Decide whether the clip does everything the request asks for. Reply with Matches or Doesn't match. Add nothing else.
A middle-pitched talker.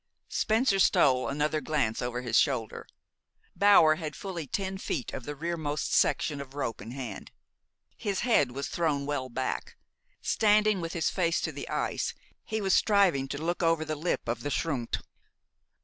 Matches